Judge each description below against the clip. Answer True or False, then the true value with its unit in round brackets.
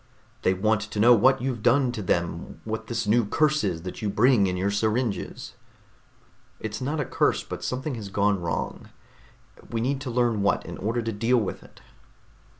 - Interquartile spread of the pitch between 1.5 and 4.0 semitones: True (3.6 semitones)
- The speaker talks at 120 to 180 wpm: False (190 wpm)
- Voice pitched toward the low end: True (110 Hz)